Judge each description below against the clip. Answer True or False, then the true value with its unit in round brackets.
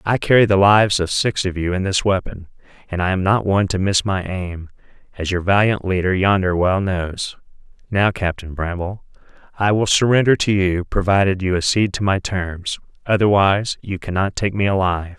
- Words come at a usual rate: True (180 wpm)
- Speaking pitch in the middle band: False (95 Hz)